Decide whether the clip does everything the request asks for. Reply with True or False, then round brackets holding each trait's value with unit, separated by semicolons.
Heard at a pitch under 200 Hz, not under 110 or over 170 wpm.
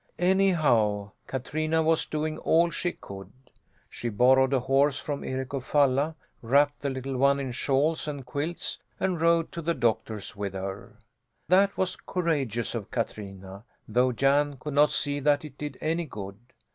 True (140 Hz; 160 wpm)